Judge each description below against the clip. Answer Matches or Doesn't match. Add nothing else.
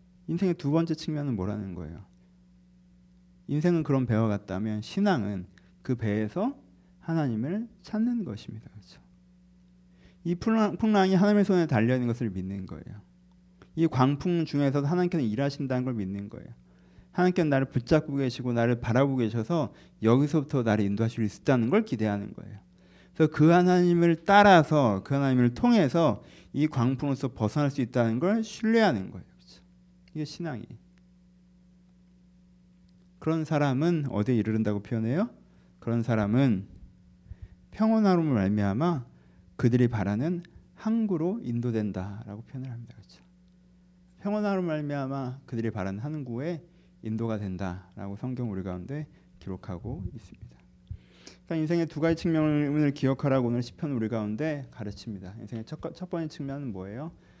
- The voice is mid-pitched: Doesn't match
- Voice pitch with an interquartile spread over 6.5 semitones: Matches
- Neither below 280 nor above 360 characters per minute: Matches